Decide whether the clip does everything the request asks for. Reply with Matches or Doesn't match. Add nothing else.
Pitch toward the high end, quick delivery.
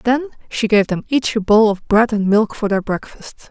Matches